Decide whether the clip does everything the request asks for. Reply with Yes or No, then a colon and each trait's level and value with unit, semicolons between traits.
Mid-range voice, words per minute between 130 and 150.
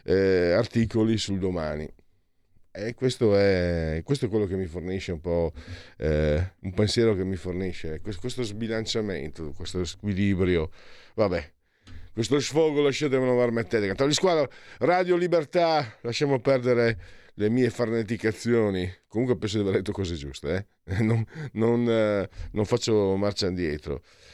No: low, 105 Hz; average, 140 wpm